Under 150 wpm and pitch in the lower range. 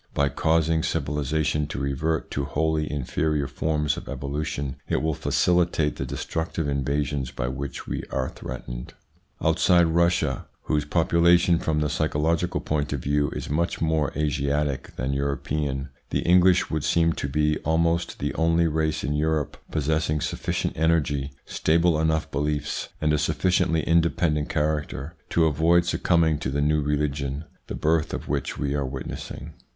No: average, 155 wpm; very low, 75 Hz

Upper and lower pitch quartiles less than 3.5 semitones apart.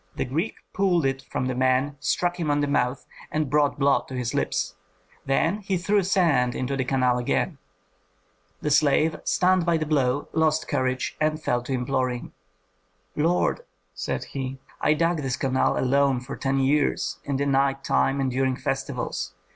Yes: average, 3.1 semitones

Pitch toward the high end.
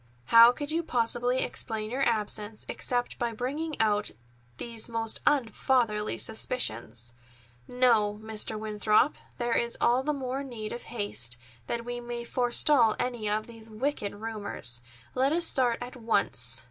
Yes: high, 235 Hz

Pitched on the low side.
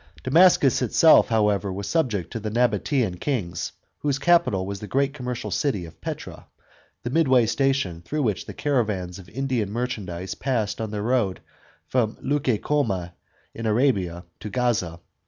Yes: low, 115 Hz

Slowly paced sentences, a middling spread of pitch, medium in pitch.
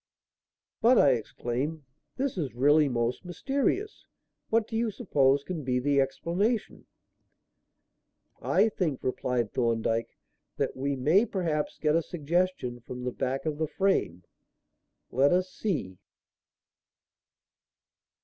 No: slow, 120 wpm; wide, 6.6 semitones; medium, 150 Hz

